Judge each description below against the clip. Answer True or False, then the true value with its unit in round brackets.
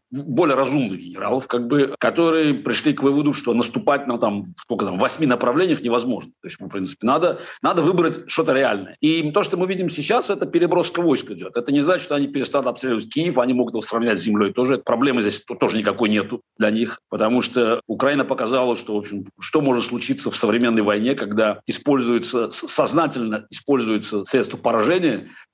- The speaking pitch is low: True (125 Hz)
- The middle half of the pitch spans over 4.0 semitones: True (5.1 semitones)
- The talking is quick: True (180 wpm)